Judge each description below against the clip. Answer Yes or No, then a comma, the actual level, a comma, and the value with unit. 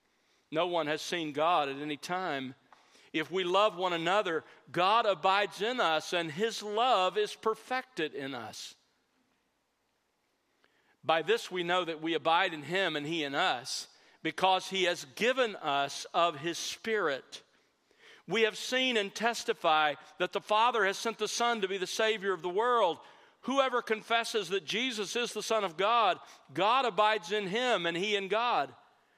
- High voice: Yes, high, 195 Hz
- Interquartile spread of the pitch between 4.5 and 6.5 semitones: Yes, average, 4.9 semitones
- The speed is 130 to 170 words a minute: Yes, average, 165 wpm